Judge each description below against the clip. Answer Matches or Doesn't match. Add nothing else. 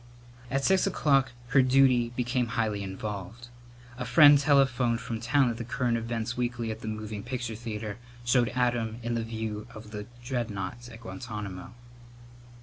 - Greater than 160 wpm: Doesn't match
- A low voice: Matches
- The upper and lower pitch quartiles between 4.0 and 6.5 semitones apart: Doesn't match